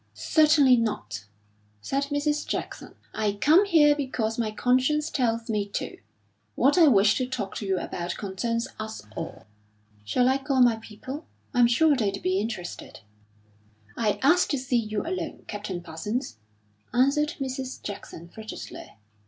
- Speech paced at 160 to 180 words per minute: No, average, 145 wpm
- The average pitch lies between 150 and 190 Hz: No, high, 240 Hz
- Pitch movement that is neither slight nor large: Yes, average, 5.0 semitones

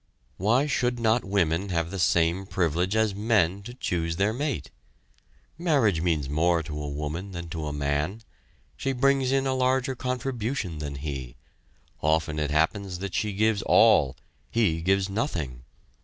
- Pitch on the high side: No, very low, 95 Hz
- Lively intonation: Yes, wide, 6.2 semitones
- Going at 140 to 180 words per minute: Yes, average, 155 wpm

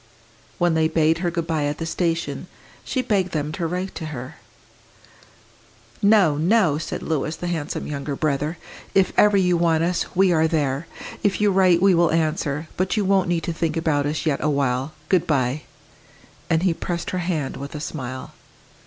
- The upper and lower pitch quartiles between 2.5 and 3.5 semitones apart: Yes, average, 3.1 semitones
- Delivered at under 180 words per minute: No, average, 185 wpm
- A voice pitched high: No, medium, 165 Hz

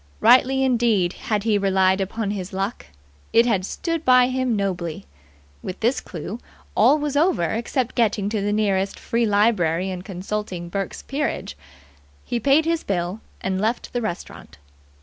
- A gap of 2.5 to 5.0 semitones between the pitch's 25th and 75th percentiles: Yes, average, 4.3 semitones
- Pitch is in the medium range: No, high, 210 Hz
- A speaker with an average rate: Yes, average, 155 wpm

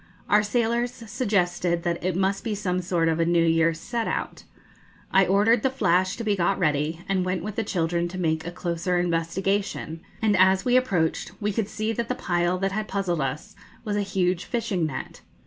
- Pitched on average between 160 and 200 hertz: Yes, medium, 185 Hz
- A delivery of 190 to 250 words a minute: Yes, average, 200 wpm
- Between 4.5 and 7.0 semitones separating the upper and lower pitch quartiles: No, average, 3.5 semitones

